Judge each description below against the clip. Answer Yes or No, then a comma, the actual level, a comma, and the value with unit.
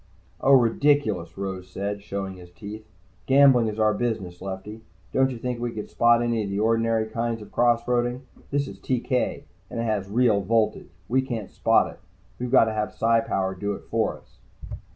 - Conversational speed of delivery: Yes, average, 195 wpm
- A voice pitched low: Yes, low, 115 Hz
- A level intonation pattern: No, average, 3.0 semitones